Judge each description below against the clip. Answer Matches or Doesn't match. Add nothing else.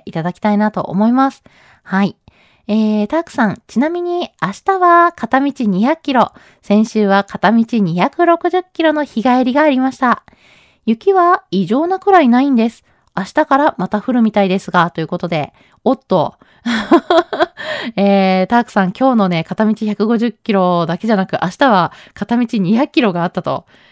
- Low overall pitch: Doesn't match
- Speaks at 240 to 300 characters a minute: Matches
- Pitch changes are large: Matches